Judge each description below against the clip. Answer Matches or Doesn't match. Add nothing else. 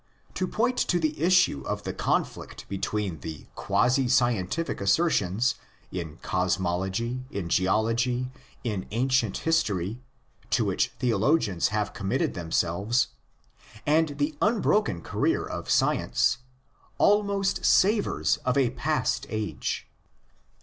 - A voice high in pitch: Doesn't match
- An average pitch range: Doesn't match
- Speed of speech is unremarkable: Doesn't match